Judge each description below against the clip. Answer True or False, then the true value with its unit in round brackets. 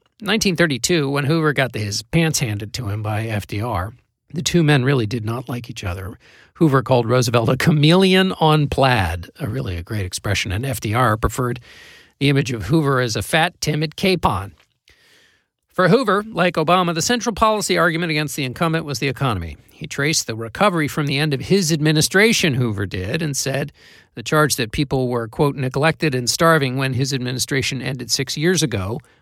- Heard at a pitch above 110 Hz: True (140 Hz)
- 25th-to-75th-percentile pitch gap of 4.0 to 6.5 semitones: True (5.2 semitones)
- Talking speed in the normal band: True (185 wpm)